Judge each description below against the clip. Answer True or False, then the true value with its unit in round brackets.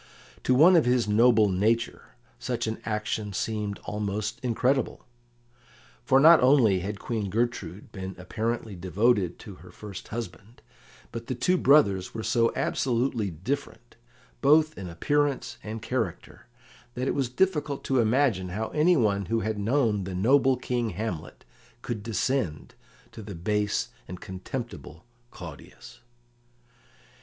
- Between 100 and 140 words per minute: True (135 wpm)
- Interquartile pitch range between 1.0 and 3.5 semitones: False (4.2 semitones)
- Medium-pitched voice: False (110 Hz)